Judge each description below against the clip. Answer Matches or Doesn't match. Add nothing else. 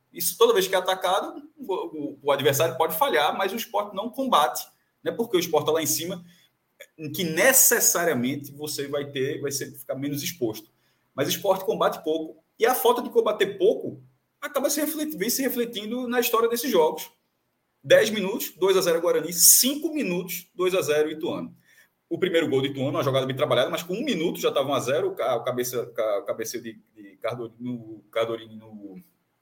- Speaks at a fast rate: Matches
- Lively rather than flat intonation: Matches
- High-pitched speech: Doesn't match